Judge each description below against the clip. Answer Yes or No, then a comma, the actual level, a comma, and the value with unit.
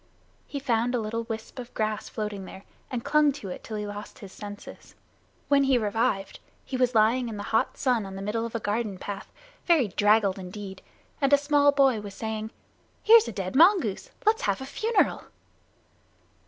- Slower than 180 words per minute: No, average, 190 wpm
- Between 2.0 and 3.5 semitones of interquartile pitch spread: No, average, 4.5 semitones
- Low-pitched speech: No, high, 225 Hz